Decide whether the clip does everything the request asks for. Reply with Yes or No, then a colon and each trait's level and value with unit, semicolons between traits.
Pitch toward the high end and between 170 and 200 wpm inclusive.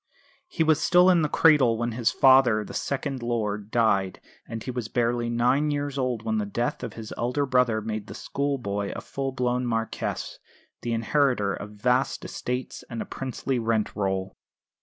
No: low, 120 Hz; average, 180 wpm